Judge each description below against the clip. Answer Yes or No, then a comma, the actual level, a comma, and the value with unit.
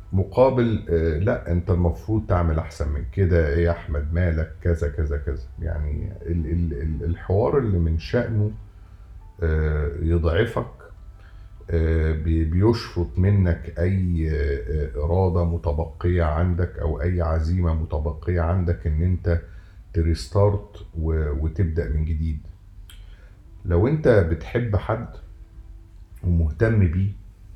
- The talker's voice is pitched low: Yes, very low, 85 Hz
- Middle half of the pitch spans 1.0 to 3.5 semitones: Yes, average, 2.7 semitones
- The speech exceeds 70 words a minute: Yes, average, 95 wpm